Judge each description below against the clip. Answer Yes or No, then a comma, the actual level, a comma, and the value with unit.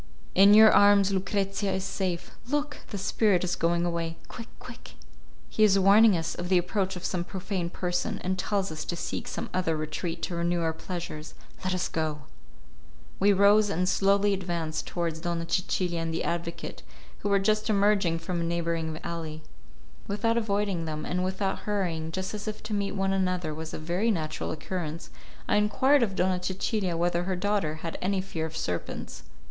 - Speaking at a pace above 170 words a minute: Yes, average, 185 wpm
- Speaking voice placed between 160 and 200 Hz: Yes, medium, 185 Hz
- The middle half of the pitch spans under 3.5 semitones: Yes, average, 3.1 semitones